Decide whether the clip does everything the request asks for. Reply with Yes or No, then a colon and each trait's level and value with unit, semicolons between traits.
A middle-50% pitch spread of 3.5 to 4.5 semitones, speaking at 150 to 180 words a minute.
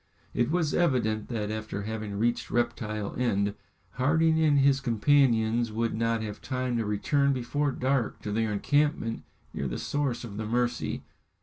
Yes: average, 4.1 semitones; average, 160 wpm